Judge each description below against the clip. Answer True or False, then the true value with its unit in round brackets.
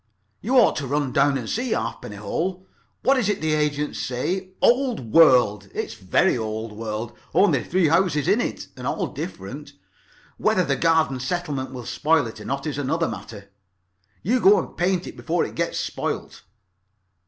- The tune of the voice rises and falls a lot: True (6.8 semitones)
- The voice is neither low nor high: True (150 Hz)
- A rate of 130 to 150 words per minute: False (175 wpm)